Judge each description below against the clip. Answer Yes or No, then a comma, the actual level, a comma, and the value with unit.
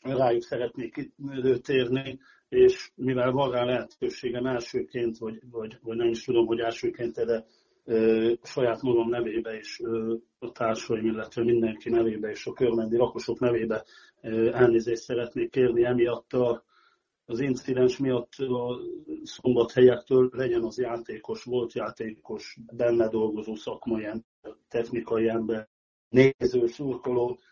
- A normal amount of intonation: No, narrow, 1.9 semitones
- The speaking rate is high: No, average, 125 wpm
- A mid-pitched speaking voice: No, low, 120 Hz